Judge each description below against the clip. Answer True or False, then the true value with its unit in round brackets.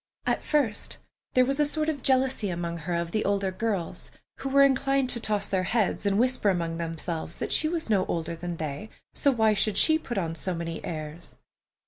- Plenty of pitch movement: True (7.3 semitones)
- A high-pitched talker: True (200 Hz)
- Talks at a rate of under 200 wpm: False (205 wpm)